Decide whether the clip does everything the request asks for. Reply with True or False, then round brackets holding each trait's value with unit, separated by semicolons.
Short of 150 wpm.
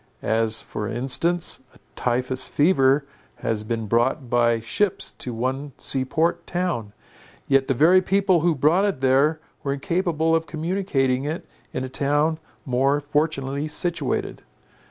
True (140 wpm)